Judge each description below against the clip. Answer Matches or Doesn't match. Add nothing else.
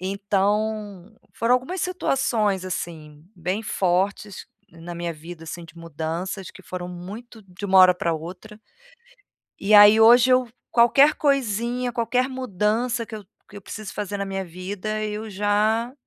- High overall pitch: Matches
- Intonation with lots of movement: Doesn't match